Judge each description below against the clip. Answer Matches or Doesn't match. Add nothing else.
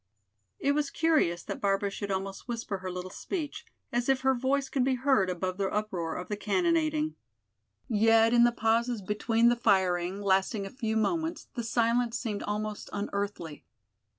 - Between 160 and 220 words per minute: Matches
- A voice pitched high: Matches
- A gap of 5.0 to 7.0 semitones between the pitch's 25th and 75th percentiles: Doesn't match